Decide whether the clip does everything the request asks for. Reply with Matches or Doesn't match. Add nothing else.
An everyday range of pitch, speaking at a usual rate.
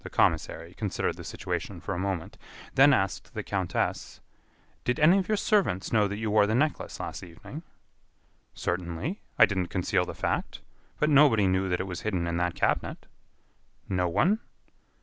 Doesn't match